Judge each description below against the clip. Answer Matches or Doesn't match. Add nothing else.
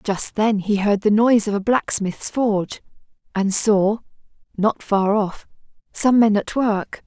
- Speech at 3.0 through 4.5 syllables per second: Matches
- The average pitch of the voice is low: Doesn't match